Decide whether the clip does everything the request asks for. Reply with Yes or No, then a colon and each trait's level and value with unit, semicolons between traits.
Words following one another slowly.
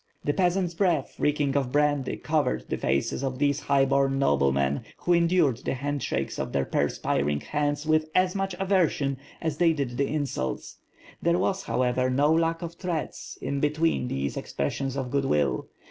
No: average, 170 wpm